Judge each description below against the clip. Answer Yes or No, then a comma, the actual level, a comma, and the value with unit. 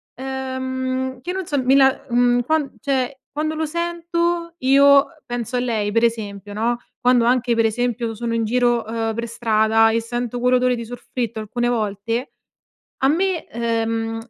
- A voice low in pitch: No, high, 245 Hz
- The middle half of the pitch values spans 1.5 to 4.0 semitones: Yes, average, 2.7 semitones